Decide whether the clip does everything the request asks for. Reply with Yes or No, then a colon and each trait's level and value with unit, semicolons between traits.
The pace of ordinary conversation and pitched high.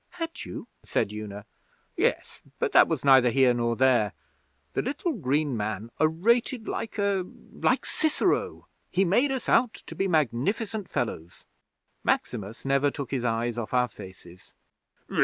No: average, 145 wpm; low, 135 Hz